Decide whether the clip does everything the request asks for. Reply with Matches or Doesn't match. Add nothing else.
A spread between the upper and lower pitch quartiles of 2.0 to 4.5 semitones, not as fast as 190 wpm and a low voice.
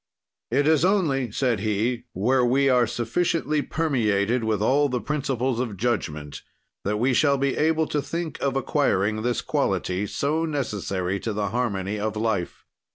Doesn't match